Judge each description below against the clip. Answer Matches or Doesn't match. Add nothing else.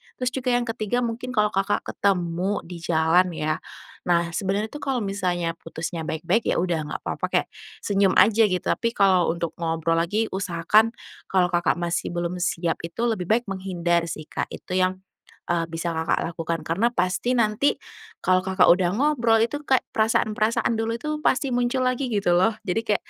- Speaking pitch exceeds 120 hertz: Matches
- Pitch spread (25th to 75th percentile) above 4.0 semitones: Matches